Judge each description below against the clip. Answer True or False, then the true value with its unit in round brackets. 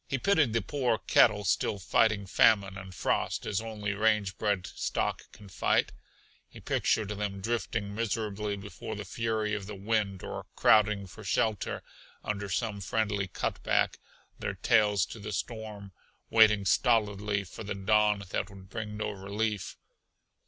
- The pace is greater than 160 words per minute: False (150 wpm)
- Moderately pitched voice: False (105 Hz)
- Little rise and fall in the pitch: True (1.8 semitones)